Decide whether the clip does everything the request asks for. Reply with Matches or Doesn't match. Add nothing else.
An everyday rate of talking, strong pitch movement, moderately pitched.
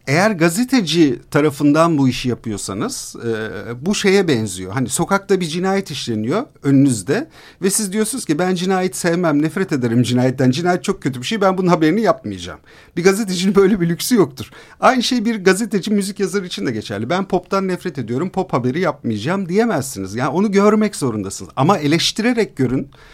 Doesn't match